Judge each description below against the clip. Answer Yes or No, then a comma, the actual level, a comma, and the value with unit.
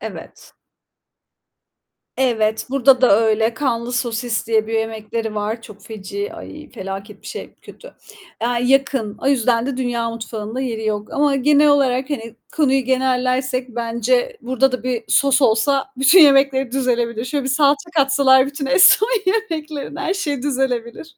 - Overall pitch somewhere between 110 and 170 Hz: No, very high, 255 Hz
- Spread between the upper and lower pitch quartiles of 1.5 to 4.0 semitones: Yes, average, 3.4 semitones